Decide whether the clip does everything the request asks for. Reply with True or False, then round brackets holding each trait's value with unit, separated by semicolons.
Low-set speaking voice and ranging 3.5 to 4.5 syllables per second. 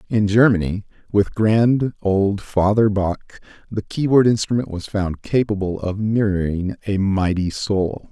True (100 Hz; 4.2 syllables/s)